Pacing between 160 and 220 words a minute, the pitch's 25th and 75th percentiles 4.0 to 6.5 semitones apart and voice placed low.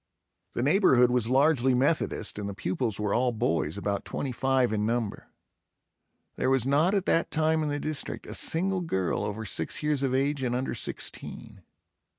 Yes: average, 175 wpm; average, 5.2 semitones; low, 130 Hz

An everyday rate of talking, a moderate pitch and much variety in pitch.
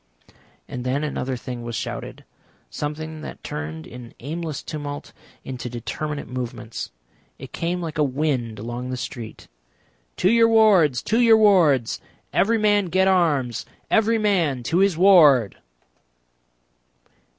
No: slow, 130 wpm; medium, 150 Hz; wide, 7.0 semitones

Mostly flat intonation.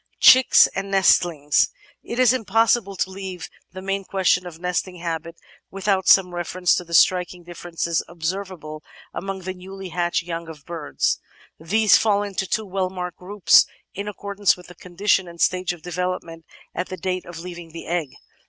Yes: narrow, 2.2 semitones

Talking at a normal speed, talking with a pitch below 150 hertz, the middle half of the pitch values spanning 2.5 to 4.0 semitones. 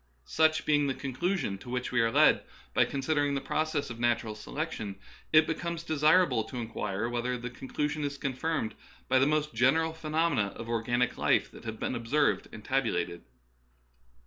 No: average, 175 wpm; low, 135 Hz; average, 4.7 semitones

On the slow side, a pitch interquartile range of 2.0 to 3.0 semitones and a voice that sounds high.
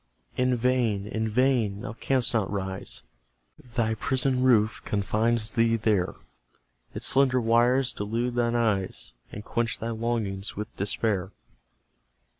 No: slow, 125 wpm; average, 2.7 semitones; low, 115 Hz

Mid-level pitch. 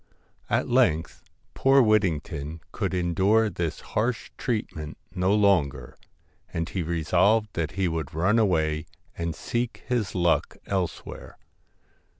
No: very low, 90 Hz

